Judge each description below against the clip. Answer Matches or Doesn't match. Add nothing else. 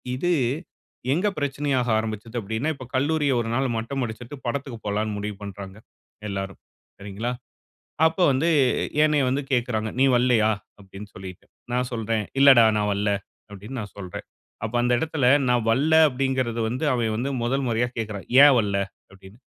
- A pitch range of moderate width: Matches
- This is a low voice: Matches